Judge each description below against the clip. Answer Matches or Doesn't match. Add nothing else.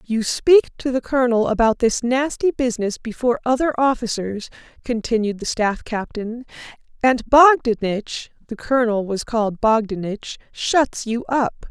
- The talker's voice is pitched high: Matches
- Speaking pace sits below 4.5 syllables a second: Matches